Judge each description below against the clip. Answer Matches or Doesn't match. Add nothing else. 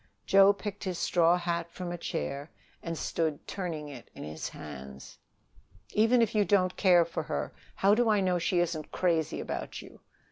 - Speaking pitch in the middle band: Matches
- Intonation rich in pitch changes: Doesn't match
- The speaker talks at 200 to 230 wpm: Doesn't match